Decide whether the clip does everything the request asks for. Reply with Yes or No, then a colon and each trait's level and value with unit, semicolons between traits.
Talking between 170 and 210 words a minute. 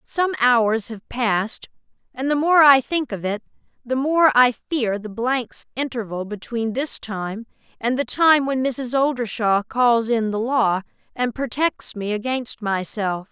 No: average, 160 wpm